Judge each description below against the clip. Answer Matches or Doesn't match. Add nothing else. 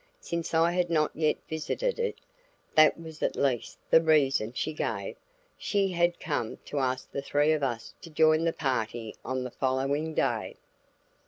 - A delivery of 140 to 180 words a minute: Matches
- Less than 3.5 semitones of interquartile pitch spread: Doesn't match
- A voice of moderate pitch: Matches